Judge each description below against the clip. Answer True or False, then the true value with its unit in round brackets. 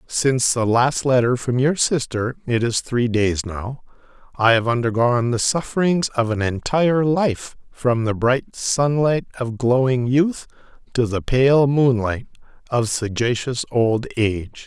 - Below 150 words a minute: True (140 wpm)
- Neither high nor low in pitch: False (125 Hz)